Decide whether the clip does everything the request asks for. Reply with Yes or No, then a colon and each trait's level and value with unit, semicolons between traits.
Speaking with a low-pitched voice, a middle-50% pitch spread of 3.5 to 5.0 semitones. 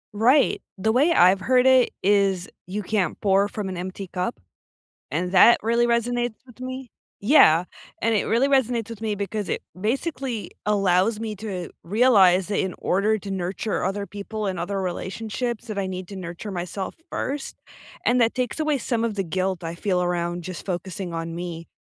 No: high, 200 Hz; average, 4.1 semitones